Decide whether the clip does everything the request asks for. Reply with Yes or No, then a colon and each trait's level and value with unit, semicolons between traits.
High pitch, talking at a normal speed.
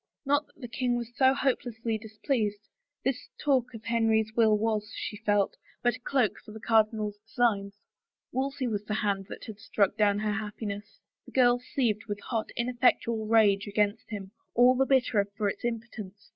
Yes: high, 220 Hz; average, 180 wpm